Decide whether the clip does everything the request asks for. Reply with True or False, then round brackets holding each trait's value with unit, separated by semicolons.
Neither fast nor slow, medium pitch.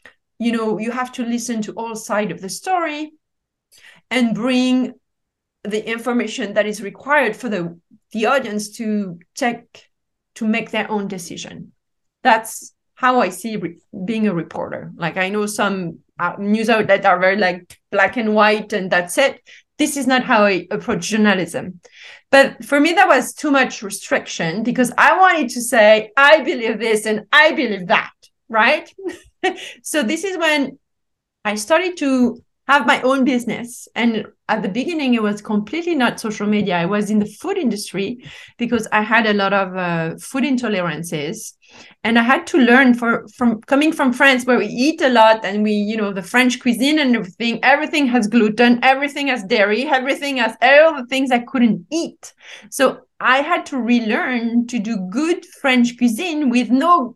False (175 wpm; 235 Hz)